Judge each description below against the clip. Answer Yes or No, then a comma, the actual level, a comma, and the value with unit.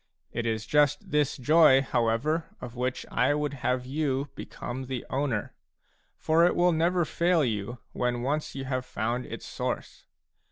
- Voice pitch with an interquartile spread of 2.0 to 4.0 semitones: Yes, average, 3.7 semitones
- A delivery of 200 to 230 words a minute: No, average, 160 wpm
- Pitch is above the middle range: No, low, 135 Hz